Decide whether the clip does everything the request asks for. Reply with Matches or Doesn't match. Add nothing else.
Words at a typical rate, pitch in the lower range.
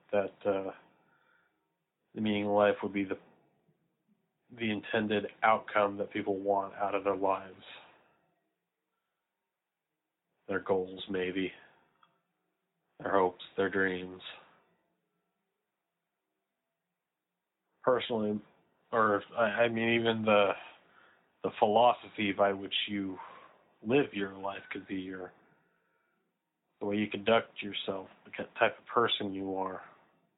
Doesn't match